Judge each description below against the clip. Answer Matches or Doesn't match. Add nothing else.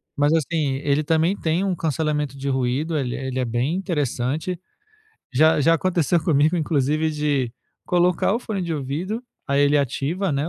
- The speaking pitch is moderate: Matches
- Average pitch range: Matches